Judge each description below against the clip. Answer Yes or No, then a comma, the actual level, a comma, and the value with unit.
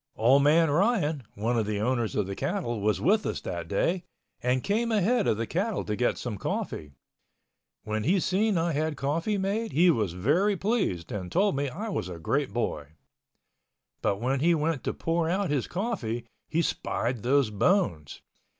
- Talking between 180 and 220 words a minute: Yes, average, 185 wpm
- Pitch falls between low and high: Yes, medium, 145 Hz